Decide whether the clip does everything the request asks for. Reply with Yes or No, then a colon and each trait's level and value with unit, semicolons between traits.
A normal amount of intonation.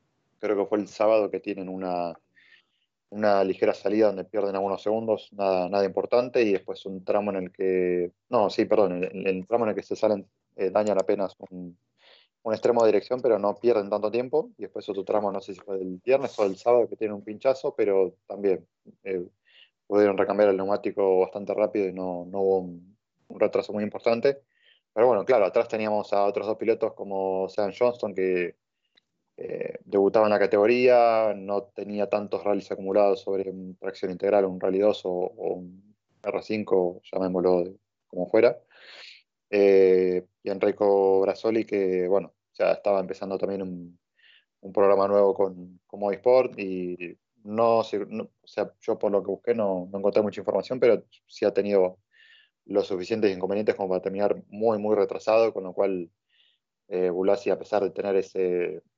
No: narrow, 2.1 semitones